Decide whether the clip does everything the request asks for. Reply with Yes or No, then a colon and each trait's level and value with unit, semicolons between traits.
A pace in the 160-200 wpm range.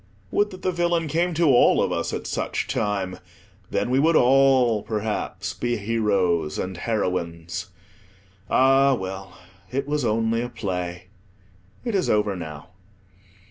No: average, 140 wpm